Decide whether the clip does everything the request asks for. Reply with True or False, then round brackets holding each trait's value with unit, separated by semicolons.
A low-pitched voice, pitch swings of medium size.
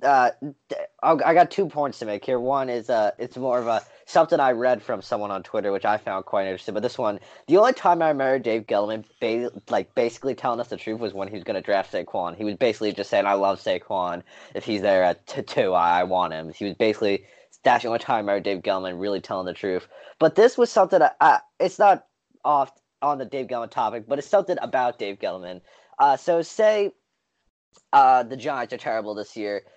False (115 Hz; 8.0 semitones)